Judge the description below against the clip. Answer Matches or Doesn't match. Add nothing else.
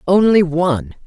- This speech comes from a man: Doesn't match